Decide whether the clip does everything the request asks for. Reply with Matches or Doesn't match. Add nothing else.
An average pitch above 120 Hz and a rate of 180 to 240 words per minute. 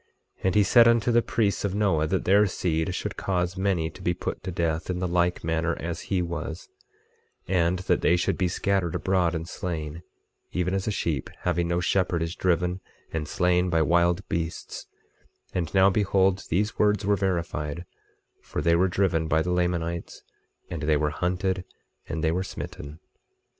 Doesn't match